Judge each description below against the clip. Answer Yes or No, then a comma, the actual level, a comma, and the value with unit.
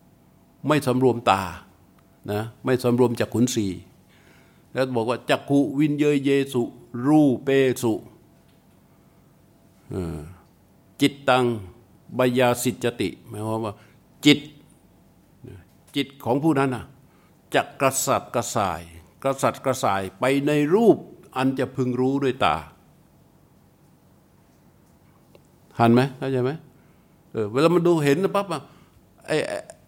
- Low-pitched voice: Yes, low, 125 Hz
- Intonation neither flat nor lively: Yes, average, 4.4 semitones